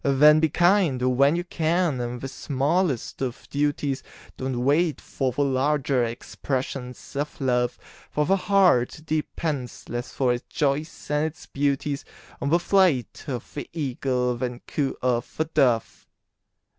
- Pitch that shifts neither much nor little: Yes, average, 3.6 semitones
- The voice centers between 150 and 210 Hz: No, medium, 140 Hz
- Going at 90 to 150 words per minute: Yes, average, 145 wpm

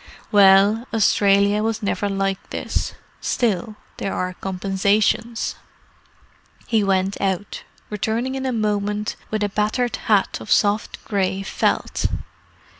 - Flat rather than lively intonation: Yes, narrow, 2.0 semitones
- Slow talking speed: Yes, slow, 115 wpm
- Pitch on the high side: Yes, high, 205 Hz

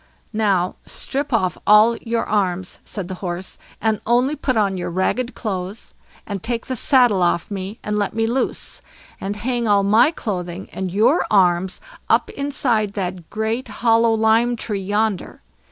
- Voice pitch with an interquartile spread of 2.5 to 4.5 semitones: Yes, average, 3.6 semitones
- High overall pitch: Yes, high, 210 Hz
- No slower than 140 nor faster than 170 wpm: Yes, average, 160 wpm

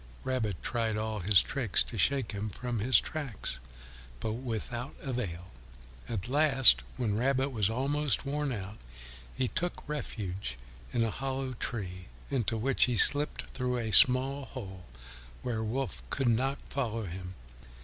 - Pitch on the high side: No, low, 120 Hz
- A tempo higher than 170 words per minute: No, average, 145 wpm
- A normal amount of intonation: Yes, average, 4.1 semitones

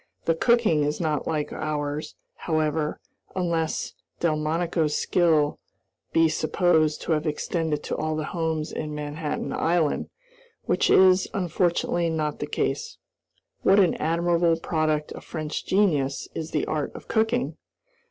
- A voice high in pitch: No, medium, 160 Hz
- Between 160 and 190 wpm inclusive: No, slow, 135 wpm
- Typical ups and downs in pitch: No, narrow, 2.2 semitones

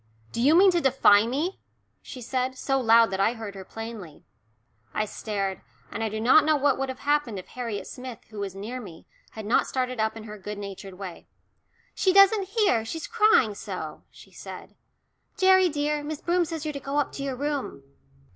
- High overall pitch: Yes, very high, 250 Hz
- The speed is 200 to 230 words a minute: Yes, fast, 205 wpm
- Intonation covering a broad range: Yes, wide, 5.8 semitones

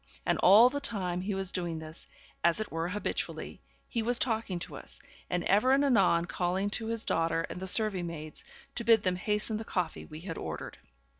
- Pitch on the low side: No, high, 190 Hz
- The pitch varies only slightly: No, average, 4.3 semitones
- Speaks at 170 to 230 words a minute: Yes, fast, 205 wpm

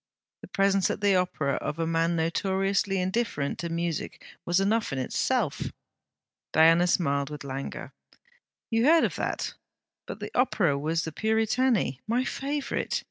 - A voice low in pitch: No, medium, 180 Hz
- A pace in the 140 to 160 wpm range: Yes, average, 145 wpm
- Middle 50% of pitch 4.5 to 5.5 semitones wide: Yes, average, 5.2 semitones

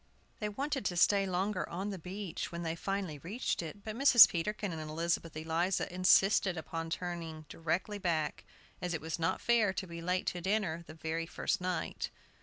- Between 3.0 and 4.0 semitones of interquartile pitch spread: Yes, average, 3.4 semitones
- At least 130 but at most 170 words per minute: No, average, 185 wpm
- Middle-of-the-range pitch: Yes, medium, 180 Hz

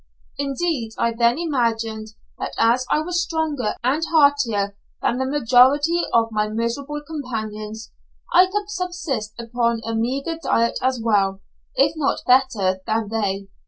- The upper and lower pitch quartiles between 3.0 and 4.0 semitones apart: No, average, 4.8 semitones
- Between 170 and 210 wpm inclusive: No, average, 140 wpm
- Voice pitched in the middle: No, high, 245 Hz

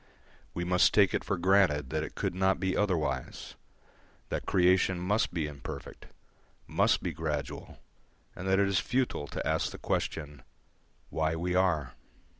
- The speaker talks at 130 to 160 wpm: Yes, average, 155 wpm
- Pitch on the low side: Yes, very low, 90 Hz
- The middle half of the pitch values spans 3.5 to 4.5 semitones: Yes, average, 3.8 semitones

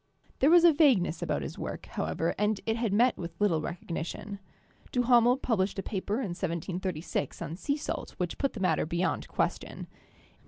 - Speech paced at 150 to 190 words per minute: Yes, average, 170 wpm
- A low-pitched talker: No, high, 195 Hz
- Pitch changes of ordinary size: No, wide, 6.0 semitones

